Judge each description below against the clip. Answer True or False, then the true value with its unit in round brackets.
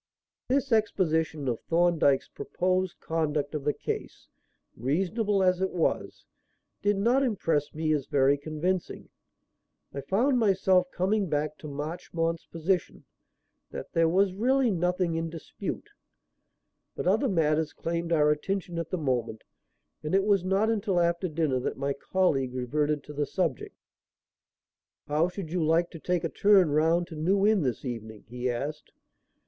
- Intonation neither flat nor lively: True (4.2 semitones)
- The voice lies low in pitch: False (165 Hz)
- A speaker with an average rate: True (150 wpm)